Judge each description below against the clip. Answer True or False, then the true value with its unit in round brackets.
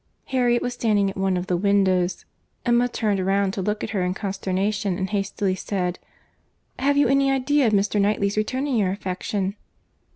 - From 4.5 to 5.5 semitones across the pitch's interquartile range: False (3.9 semitones)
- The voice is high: True (200 Hz)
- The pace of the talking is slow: False (175 wpm)